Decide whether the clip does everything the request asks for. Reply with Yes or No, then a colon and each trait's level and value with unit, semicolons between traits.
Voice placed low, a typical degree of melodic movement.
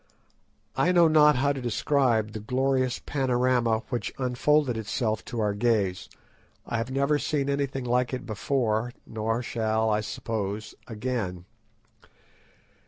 Yes: low, 120 Hz; average, 3.5 semitones